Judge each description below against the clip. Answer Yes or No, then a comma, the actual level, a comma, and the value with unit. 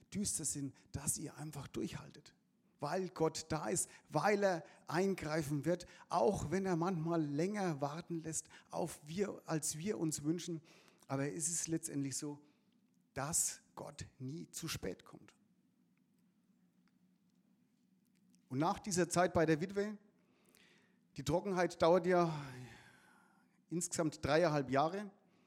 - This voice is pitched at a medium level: Yes, medium, 170 Hz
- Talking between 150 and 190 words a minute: No, slow, 125 wpm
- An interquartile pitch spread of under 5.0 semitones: Yes, average, 4.2 semitones